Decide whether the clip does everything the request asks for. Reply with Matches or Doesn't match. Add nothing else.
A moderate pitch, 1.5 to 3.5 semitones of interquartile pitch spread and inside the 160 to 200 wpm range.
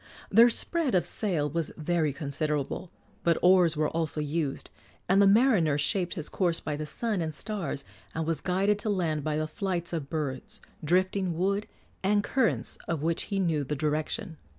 Doesn't match